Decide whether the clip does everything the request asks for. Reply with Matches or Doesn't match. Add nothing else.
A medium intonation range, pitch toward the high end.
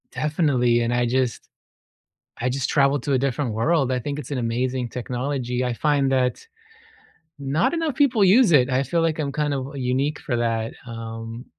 Doesn't match